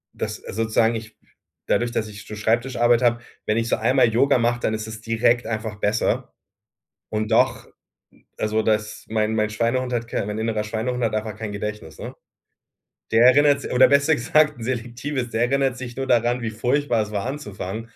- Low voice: Yes, low, 115 Hz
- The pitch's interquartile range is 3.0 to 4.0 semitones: No, narrow, 2.4 semitones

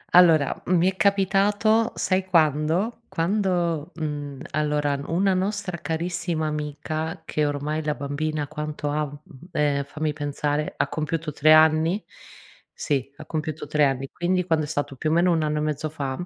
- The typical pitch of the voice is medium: Yes, medium, 155 Hz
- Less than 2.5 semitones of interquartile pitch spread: No, average, 2.9 semitones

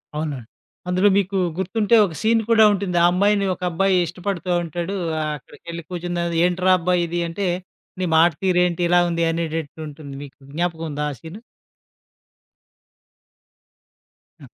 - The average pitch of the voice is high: No, medium, 175 Hz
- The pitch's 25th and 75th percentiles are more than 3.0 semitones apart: No, narrow, 2.5 semitones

